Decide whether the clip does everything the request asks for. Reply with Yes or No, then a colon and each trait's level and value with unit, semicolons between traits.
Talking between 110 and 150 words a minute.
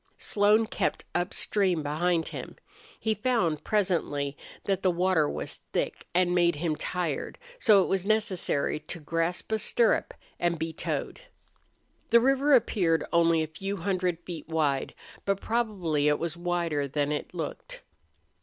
Yes: average, 145 wpm